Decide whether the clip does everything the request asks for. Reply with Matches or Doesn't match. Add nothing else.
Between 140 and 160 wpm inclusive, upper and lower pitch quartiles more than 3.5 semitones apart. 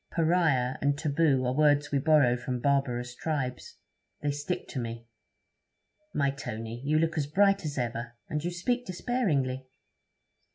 Matches